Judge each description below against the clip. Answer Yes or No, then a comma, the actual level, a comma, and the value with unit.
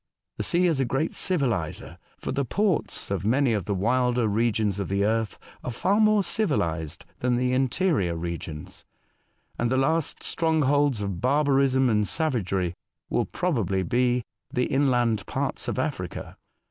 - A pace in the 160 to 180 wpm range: No, average, 150 wpm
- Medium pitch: No, low, 125 Hz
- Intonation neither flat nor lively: No, wide, 5.8 semitones